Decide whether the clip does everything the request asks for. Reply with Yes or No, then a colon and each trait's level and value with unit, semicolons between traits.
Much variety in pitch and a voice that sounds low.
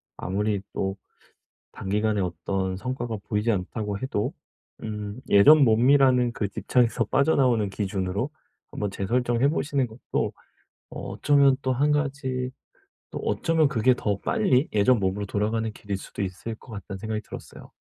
No: average, 4.2 semitones; low, 110 Hz